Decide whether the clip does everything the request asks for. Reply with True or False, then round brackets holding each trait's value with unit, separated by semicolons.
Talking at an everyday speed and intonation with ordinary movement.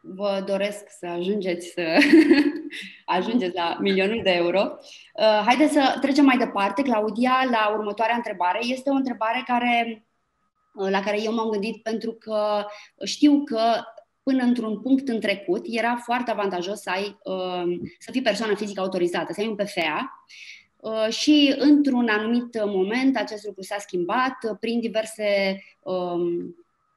True (135 wpm; 4.3 semitones)